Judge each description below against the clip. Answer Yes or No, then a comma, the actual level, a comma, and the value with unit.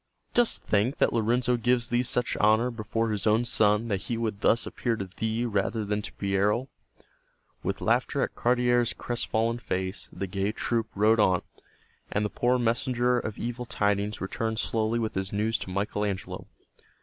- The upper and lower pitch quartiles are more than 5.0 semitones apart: No, average, 2.7 semitones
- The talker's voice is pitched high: No, low, 110 Hz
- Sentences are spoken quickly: No, average, 175 wpm